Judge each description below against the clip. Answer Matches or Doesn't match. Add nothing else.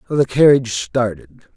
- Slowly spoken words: Matches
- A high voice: Doesn't match